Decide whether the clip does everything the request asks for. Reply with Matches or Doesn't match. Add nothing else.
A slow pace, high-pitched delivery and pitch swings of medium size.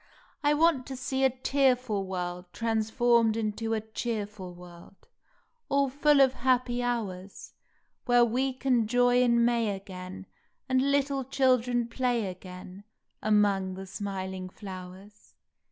Matches